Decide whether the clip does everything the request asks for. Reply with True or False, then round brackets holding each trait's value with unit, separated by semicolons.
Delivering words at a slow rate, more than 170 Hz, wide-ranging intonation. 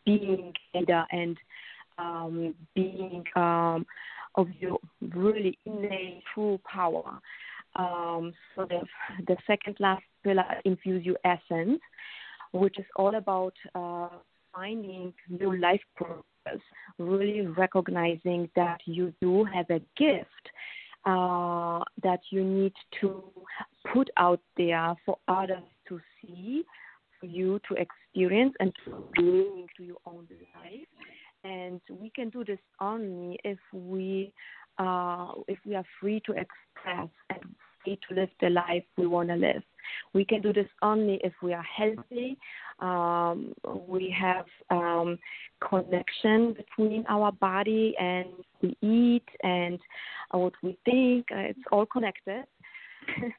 False (125 wpm; 190 Hz; 2.7 semitones)